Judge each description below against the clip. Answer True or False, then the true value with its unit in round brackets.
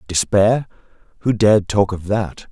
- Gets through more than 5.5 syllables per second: False (4.5 syllables/s)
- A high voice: False (105 Hz)